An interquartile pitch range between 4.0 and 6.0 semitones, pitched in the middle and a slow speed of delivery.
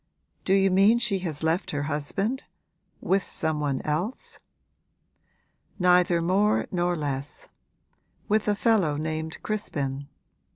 Yes: average, 4.8 semitones; medium, 175 Hz; slow, 120 wpm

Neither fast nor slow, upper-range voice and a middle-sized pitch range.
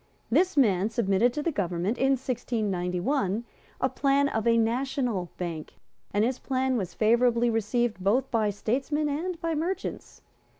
Yes: average, 145 wpm; high, 240 Hz; average, 4.8 semitones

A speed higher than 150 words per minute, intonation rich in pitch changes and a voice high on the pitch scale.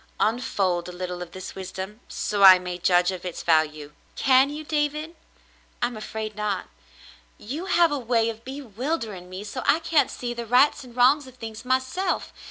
Yes: average, 185 wpm; wide, 6.2 semitones; high, 225 Hz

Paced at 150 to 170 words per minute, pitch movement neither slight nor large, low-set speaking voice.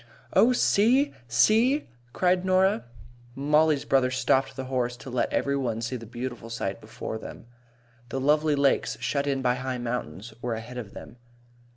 Yes: average, 165 wpm; average, 3.9 semitones; low, 130 Hz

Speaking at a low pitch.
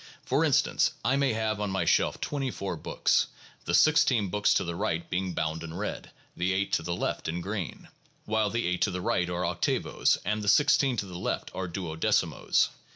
Yes: very low, 95 Hz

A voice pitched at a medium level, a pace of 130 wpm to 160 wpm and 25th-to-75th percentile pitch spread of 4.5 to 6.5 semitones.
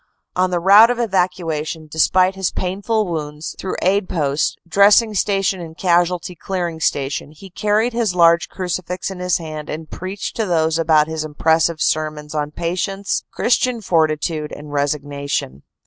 No: medium, 170 Hz; average, 155 wpm; average, 3.7 semitones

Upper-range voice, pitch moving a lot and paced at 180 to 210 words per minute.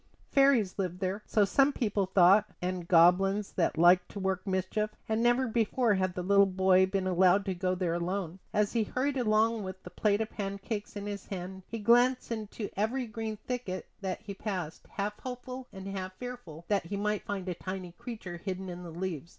No: high, 195 Hz; average, 2.9 semitones; average, 200 wpm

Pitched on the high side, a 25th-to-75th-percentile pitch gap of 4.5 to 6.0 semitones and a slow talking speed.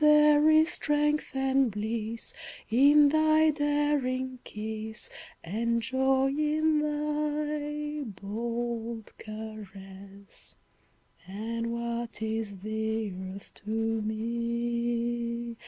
Yes: high, 235 Hz; average, 5.1 semitones; slow, 85 wpm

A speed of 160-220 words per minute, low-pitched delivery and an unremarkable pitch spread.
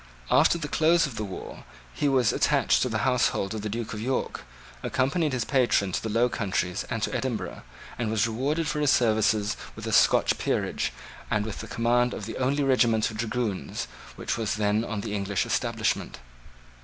Yes: average, 190 wpm; low, 115 Hz; average, 3.4 semitones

